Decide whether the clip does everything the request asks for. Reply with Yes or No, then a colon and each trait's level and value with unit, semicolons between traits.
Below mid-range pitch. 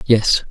Yes: low, 110 Hz